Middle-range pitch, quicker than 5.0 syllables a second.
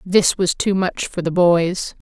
No: medium, 180 Hz; 3.7 syllables/s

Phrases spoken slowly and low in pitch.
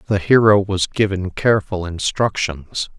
Yes: slow, 120 wpm; very low, 95 Hz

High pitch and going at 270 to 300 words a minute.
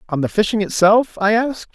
No: high, 210 Hz; fast, 205 wpm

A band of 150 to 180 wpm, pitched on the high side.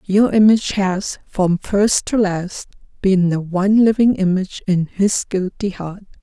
Yes: average, 155 wpm; high, 195 Hz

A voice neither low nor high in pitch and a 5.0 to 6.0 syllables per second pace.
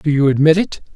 No: medium, 150 Hz; 6.2 syllables/s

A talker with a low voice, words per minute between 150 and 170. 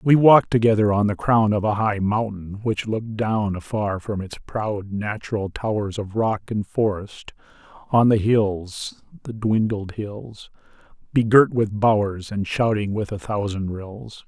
Yes: low, 105 Hz; average, 160 wpm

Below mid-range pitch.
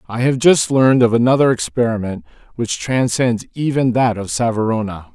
Yes: low, 115 Hz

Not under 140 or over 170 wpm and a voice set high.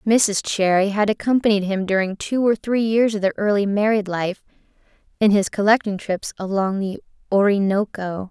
Yes: average, 160 wpm; high, 205 Hz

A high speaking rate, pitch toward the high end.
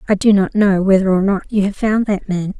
Yes: fast, 275 wpm; high, 195 Hz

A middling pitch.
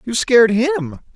No: high, 235 Hz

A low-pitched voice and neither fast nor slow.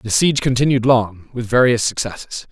Yes: low, 120 Hz; average, 165 wpm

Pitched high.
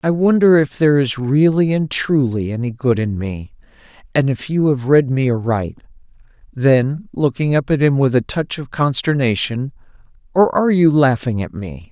No: low, 135 Hz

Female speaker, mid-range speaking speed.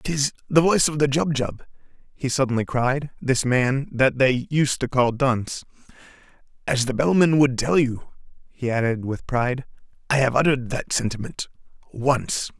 No: male; average, 155 wpm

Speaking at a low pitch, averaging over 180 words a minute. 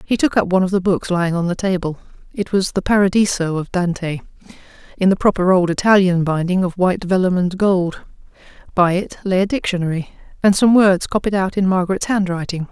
No: medium, 185 Hz; average, 200 wpm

